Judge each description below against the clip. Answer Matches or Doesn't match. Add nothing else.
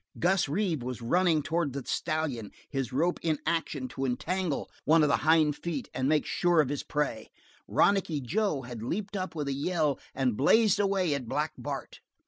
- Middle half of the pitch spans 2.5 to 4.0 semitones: Doesn't match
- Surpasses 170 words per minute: Matches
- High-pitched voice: Doesn't match